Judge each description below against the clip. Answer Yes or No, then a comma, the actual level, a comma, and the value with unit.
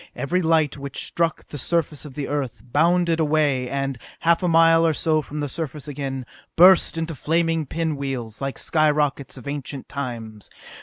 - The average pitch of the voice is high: No, medium, 150 Hz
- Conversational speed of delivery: Yes, average, 170 wpm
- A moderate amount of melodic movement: Yes, average, 3.1 semitones